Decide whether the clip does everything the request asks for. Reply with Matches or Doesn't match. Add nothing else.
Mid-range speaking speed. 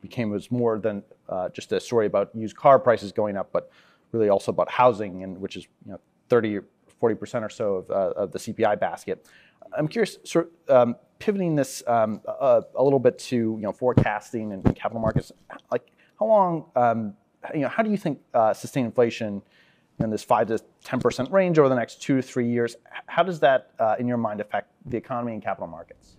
Doesn't match